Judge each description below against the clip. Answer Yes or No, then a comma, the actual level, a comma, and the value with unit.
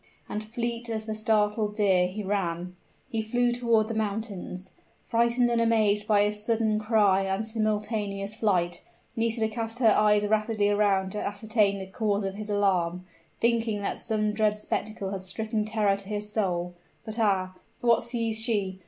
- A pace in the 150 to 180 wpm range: Yes, average, 165 wpm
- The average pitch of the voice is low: No, high, 210 Hz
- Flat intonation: Yes, narrow, 1.9 semitones